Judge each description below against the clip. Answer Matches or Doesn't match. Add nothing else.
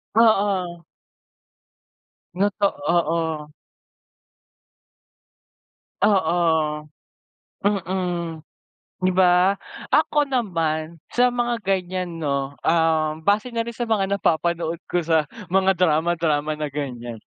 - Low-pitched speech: Doesn't match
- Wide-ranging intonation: Doesn't match